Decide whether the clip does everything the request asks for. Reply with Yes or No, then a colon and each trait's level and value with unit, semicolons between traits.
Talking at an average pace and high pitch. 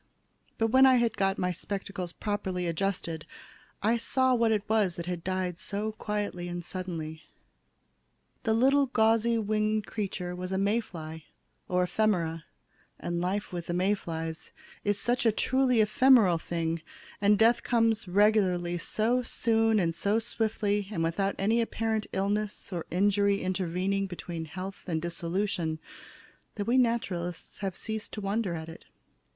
Yes: average, 150 wpm; high, 200 Hz